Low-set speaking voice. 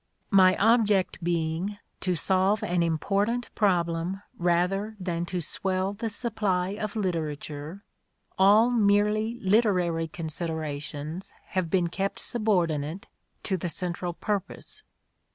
No: medium, 185 Hz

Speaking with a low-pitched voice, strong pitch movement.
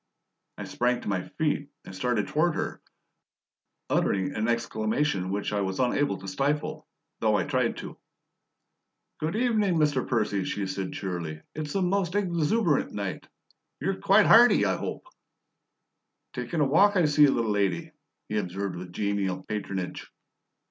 Yes: low, 120 Hz; wide, 8.4 semitones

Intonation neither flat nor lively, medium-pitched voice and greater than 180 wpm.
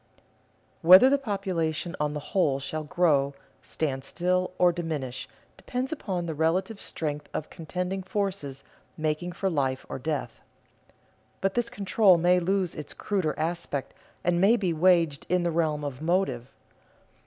No: average, 3.9 semitones; medium, 170 Hz; average, 150 wpm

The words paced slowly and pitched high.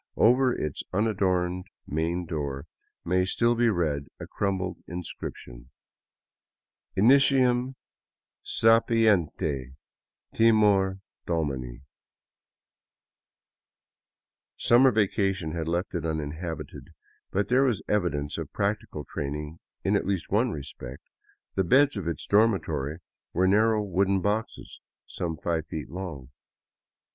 No: slow, 110 wpm; very low, 90 Hz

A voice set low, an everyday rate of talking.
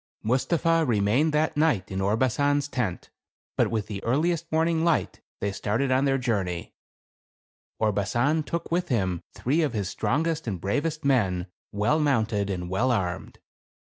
Yes: low, 125 Hz; average, 150 wpm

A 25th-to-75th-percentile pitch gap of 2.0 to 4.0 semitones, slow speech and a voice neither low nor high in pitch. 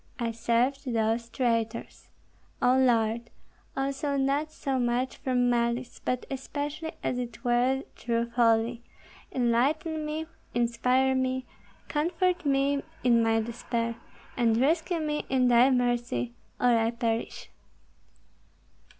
No: narrow, 2.6 semitones; slow, 115 wpm; high, 245 Hz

